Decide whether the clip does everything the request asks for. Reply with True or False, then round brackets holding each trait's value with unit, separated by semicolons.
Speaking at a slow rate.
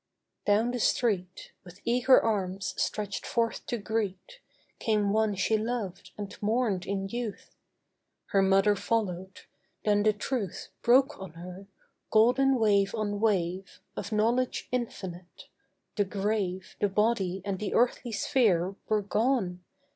True (130 wpm)